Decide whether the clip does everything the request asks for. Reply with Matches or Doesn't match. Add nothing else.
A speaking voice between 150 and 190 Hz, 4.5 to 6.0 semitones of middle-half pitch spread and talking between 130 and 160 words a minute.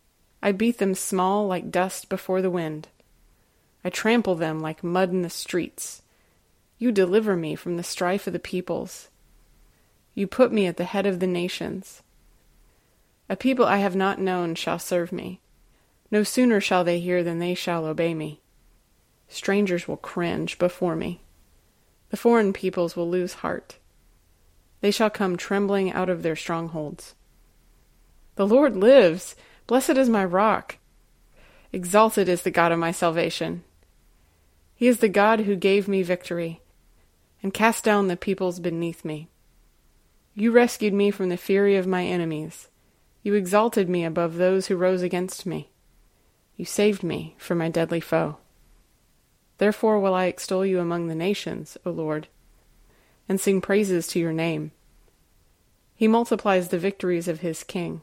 Doesn't match